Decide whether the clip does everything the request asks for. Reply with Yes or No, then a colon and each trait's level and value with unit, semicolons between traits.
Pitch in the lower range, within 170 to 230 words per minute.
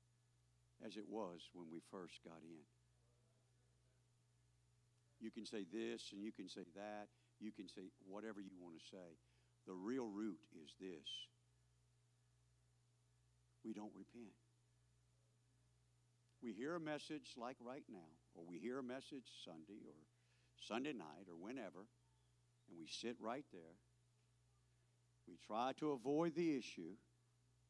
No: very low, 90 Hz; slow, 135 wpm